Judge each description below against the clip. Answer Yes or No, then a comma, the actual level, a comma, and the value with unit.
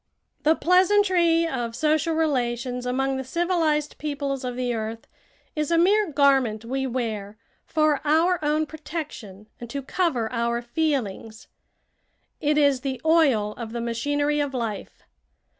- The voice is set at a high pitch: Yes, very high, 275 Hz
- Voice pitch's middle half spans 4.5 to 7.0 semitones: Yes, average, 4.8 semitones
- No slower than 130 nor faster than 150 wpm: Yes, average, 140 wpm